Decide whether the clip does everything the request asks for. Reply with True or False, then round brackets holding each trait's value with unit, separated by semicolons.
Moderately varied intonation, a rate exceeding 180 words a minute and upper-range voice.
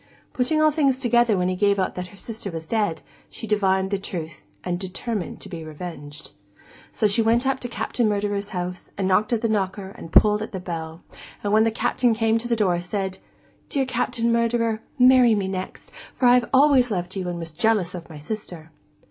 True (4.4 semitones; 205 wpm; 205 Hz)